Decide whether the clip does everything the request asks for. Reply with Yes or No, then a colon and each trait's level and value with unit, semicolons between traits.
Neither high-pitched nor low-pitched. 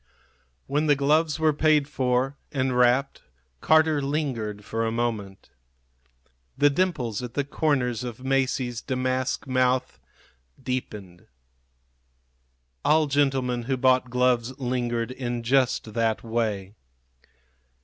No: low, 130 Hz